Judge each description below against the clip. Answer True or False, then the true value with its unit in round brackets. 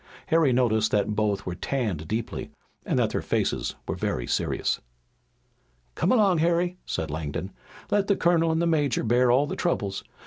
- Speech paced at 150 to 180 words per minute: True (170 wpm)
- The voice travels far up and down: True (8.5 semitones)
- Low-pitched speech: True (130 Hz)